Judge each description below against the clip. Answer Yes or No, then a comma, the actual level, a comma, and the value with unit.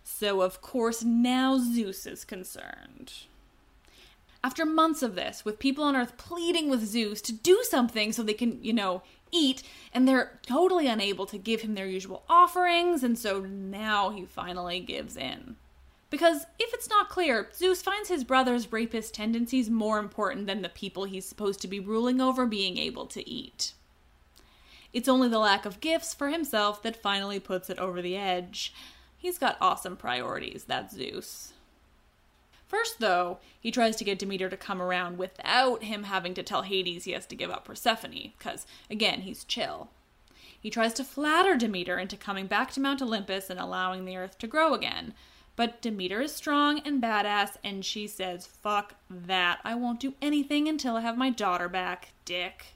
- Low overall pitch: No, high, 225 Hz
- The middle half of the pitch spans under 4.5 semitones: No, average, 5.3 semitones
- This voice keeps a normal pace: Yes, average, 180 wpm